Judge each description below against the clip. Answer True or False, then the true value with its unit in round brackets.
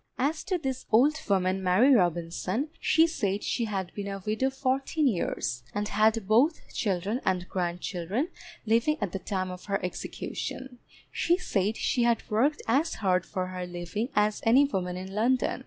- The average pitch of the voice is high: True (210 Hz)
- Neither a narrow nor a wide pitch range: False (5.8 semitones)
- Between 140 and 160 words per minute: False (170 wpm)